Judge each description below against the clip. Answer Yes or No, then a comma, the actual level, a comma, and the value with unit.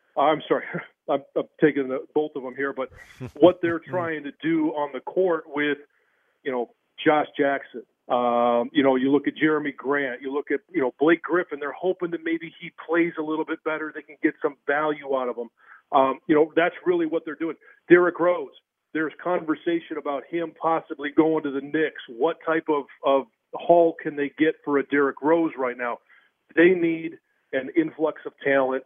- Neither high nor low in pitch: Yes, medium, 155 Hz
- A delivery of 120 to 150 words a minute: No, average, 200 wpm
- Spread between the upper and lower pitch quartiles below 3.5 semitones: Yes, average, 2.9 semitones